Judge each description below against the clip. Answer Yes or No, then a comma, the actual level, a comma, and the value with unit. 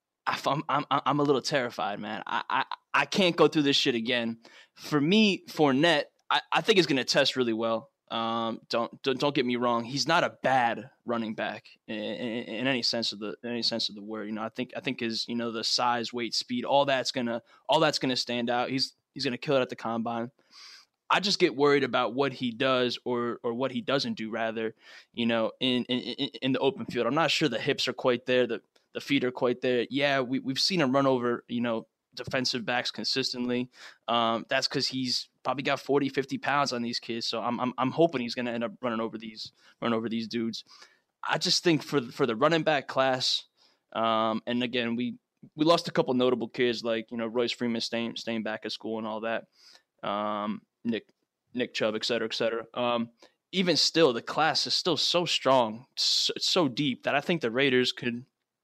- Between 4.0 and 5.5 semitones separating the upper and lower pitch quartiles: No, average, 2.8 semitones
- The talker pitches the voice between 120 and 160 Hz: Yes, low, 125 Hz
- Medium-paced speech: No, fast, 225 wpm